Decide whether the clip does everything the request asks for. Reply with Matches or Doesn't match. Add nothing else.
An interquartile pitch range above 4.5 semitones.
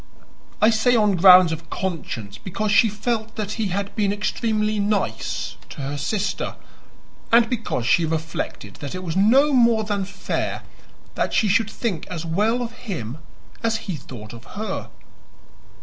Matches